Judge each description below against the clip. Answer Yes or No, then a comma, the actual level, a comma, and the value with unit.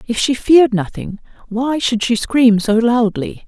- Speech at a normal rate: Yes, average, 175 wpm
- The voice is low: No, high, 235 Hz